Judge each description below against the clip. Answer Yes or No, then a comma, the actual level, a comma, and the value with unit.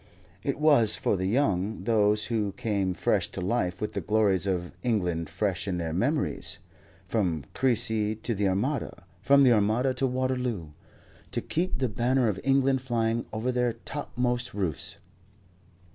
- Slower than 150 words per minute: No, average, 155 wpm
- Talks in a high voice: No, low, 110 Hz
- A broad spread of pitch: No, average, 4.5 semitones